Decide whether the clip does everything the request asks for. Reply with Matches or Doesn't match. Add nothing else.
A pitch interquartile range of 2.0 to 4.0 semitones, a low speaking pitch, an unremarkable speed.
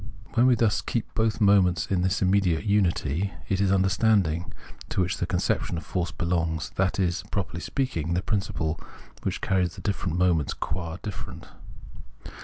Matches